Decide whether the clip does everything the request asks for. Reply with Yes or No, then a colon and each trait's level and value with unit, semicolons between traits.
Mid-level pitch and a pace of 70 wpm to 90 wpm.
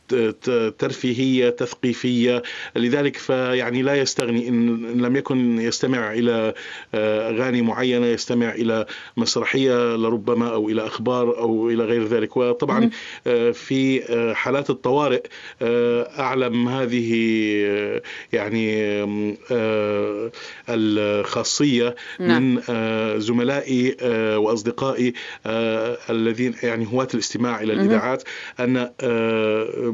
No: low, 120 Hz; average, 85 wpm